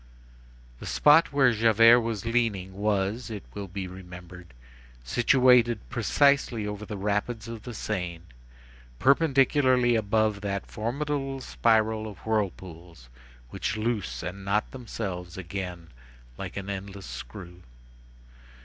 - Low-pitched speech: Yes, low, 105 Hz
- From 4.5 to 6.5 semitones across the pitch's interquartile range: No, average, 4.0 semitones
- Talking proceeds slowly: Yes, slow, 115 wpm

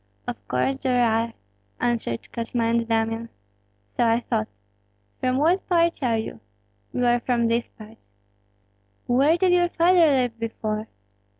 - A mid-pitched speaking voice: No, high, 235 Hz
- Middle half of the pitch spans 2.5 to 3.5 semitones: Yes, average, 3.0 semitones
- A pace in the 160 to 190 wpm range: No, average, 140 wpm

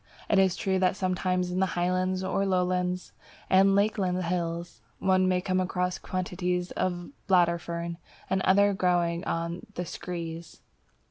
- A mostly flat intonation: Yes, narrow, 1.2 semitones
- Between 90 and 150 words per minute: Yes, average, 140 wpm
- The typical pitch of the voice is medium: Yes, medium, 180 Hz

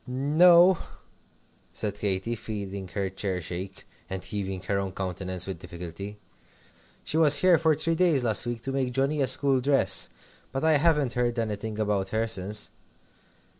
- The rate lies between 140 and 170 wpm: Yes, average, 160 wpm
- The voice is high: No, low, 110 Hz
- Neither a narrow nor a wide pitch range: No, wide, 6.4 semitones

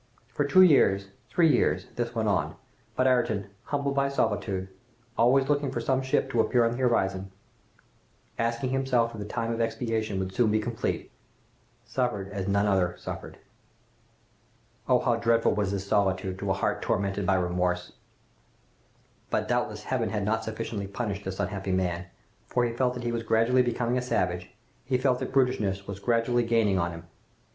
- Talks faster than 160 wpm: Yes, average, 175 wpm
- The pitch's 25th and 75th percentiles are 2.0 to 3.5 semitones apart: No, average, 4.1 semitones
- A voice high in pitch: No, low, 115 Hz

